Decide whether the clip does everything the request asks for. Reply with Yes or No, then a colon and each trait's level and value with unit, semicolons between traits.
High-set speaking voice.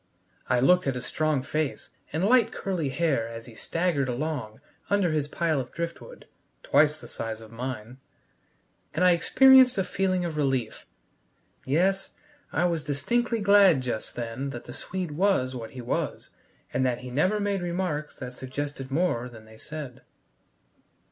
No: medium, 150 Hz